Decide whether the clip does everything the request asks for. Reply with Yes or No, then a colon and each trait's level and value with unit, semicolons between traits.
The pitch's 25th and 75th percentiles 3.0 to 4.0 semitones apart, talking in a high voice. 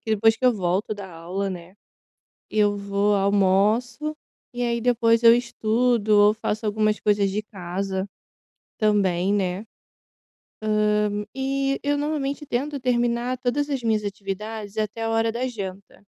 Yes: average, 3.4 semitones; high, 215 Hz